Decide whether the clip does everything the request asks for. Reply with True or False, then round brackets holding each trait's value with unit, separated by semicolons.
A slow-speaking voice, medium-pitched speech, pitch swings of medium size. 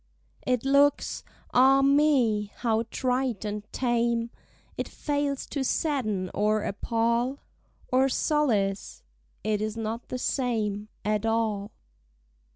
False (105 wpm; 235 Hz; 3.9 semitones)